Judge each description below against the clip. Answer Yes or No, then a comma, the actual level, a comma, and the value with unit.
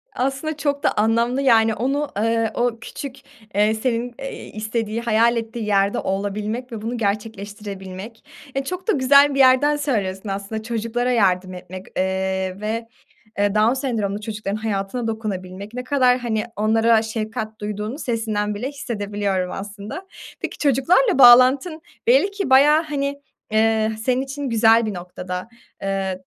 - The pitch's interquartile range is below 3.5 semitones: No, average, 3.9 semitones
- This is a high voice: Yes, high, 225 Hz